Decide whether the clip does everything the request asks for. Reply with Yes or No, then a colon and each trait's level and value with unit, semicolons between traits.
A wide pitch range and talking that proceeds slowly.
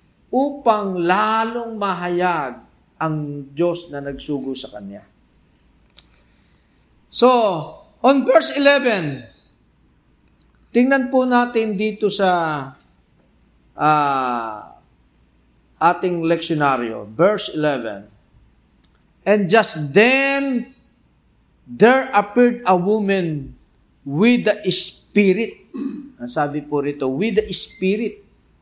Yes: wide, 8.0 semitones; slow, 85 wpm